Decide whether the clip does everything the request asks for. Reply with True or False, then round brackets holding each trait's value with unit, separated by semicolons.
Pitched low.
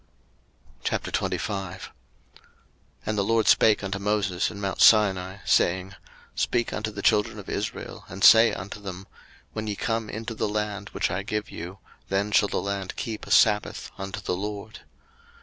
True (100 Hz)